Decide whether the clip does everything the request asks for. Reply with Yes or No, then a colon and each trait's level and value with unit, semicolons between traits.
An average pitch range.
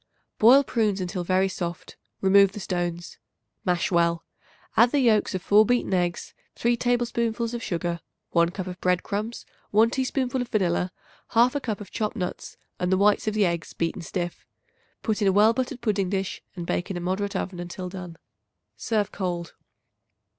Yes: average, 4.2 semitones